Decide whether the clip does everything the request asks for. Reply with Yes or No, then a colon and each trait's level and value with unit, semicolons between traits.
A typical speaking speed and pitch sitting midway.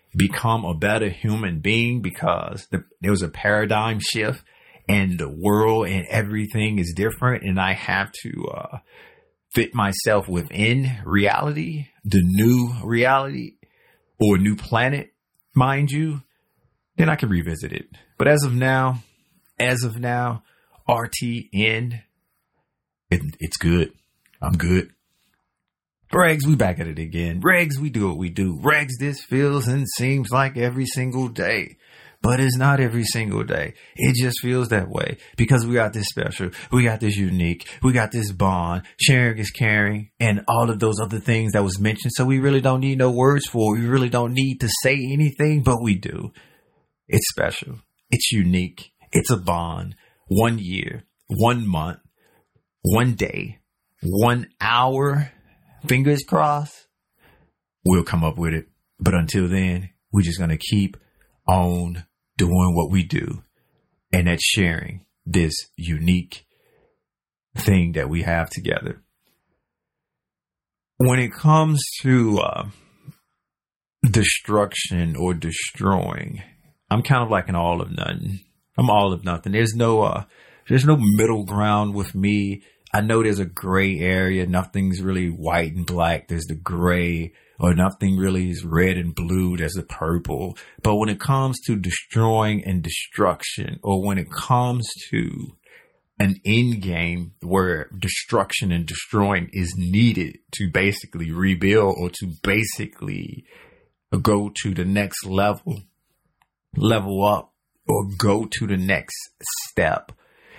No: average, 145 wpm; low, 105 Hz